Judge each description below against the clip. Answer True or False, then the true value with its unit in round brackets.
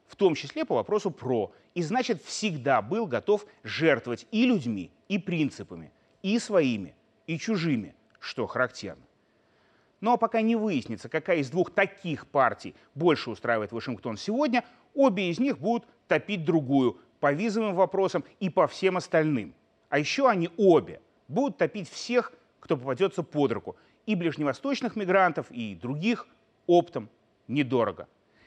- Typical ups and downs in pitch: False (8.0 semitones)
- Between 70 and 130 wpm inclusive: False (140 wpm)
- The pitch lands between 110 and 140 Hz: False (180 Hz)